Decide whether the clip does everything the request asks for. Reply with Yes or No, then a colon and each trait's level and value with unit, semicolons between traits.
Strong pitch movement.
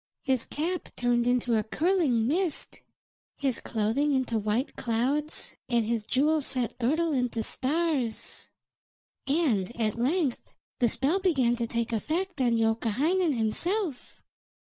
No: average, 5.0 semitones